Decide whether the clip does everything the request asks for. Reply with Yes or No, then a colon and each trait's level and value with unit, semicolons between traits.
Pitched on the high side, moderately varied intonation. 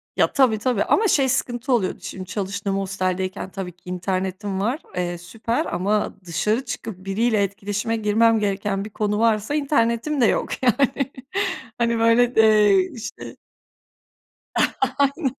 Yes: high, 215 Hz; average, 3.5 semitones